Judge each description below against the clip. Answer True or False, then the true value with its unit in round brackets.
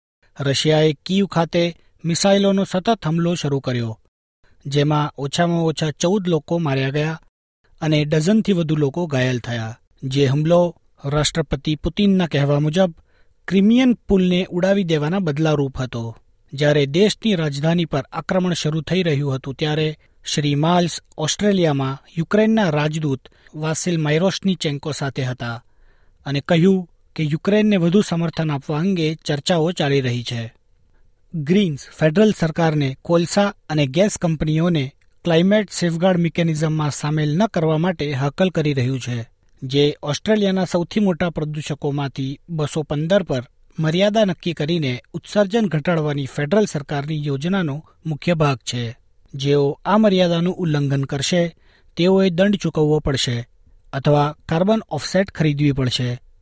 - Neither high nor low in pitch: True (155 Hz)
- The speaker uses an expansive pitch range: False (4.0 semitones)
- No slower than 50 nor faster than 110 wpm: False (125 wpm)